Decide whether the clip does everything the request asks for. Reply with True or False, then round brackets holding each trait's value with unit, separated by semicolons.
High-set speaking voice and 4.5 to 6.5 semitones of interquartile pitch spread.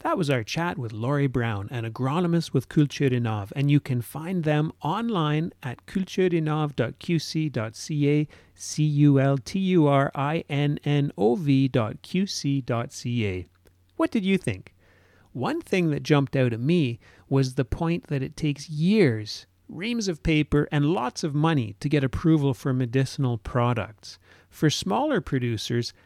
False (140 Hz; 5.0 semitones)